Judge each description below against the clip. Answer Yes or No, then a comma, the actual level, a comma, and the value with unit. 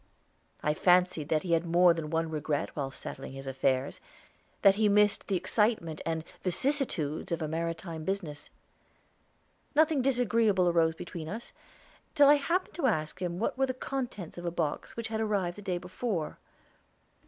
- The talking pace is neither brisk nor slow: Yes, average, 165 wpm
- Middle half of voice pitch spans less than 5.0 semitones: No, wide, 5.4 semitones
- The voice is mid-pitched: Yes, medium, 175 Hz